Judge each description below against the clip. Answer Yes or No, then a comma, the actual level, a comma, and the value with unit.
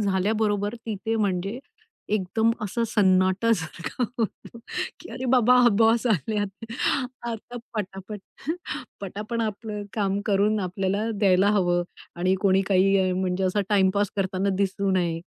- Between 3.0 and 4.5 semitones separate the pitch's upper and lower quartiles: No, narrow, 2.4 semitones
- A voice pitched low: No, high, 200 Hz